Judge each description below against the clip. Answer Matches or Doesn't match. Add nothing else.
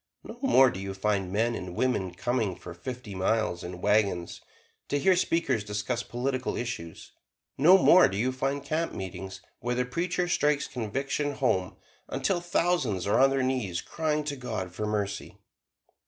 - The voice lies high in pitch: Doesn't match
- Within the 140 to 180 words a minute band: Matches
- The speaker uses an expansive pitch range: Matches